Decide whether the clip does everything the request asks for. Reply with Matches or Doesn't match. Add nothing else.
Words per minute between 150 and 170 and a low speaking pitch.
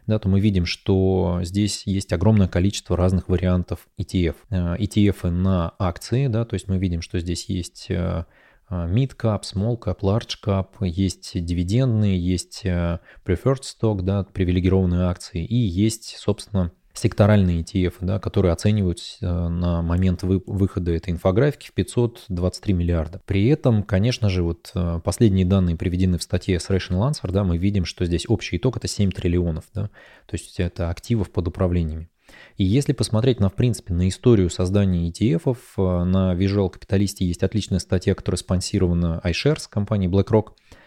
Matches